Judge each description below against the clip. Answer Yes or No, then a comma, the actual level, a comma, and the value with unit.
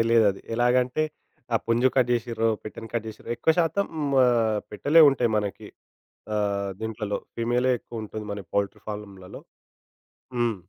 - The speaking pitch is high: No, low, 115 Hz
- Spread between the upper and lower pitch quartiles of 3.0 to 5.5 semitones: No, narrow, 2.6 semitones